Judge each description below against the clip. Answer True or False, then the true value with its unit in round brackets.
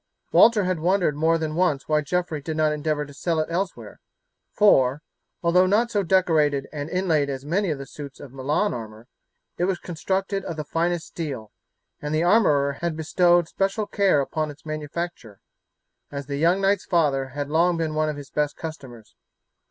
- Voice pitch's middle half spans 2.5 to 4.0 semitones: True (3.7 semitones)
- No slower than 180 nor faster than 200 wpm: True (185 wpm)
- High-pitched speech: False (155 Hz)